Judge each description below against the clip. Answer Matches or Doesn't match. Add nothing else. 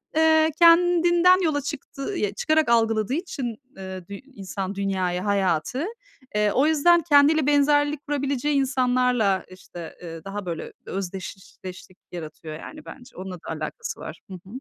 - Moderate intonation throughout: Doesn't match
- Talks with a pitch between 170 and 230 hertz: Doesn't match